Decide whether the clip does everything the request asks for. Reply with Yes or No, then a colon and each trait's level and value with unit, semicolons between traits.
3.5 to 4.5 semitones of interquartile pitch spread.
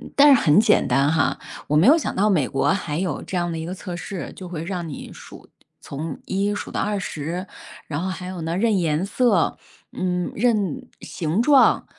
Yes: average, 4.0 semitones